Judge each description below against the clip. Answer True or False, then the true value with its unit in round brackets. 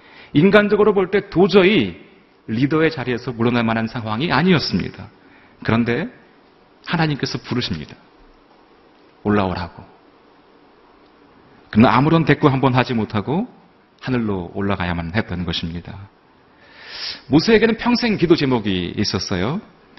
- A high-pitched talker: False (125 Hz)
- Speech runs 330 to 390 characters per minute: False (280 characters per minute)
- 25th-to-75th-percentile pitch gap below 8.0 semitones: False (8.8 semitones)